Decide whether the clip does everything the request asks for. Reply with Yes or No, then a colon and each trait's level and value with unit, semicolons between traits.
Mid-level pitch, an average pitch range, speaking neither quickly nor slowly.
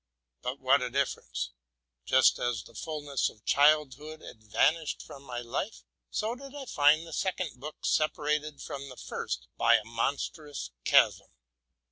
Yes: medium, 145 Hz; average, 3.8 semitones; average, 155 wpm